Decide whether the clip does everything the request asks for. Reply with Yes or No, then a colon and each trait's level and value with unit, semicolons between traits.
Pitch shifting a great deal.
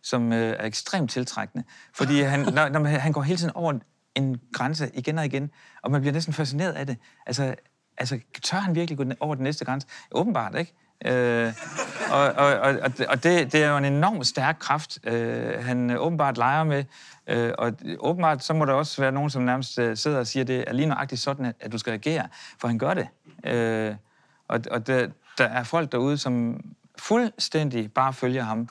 No: average, 3.9 semitones